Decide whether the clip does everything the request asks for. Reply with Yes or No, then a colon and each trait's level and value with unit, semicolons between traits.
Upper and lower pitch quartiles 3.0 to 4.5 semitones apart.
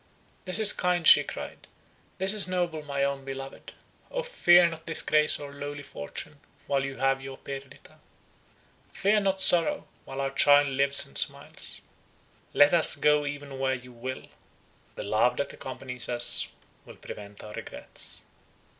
Yes: average, 3.6 semitones